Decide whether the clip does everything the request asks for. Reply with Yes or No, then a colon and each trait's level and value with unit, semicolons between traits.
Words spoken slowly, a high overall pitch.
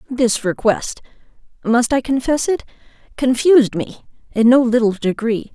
Yes: slow, 110 wpm; high, 240 Hz